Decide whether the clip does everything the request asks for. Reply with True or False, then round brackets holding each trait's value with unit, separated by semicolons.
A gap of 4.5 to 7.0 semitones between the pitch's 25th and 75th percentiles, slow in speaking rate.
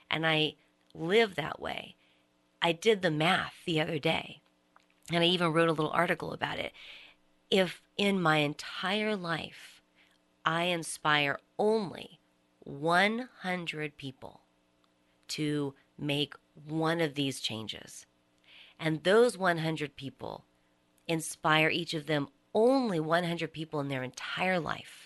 True (5.4 semitones; 125 wpm)